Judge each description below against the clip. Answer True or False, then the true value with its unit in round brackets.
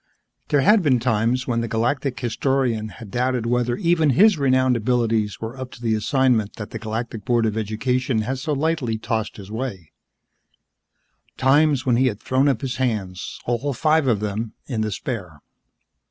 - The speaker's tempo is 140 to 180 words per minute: True (170 wpm)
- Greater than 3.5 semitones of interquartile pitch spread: False (3.1 semitones)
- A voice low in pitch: True (120 Hz)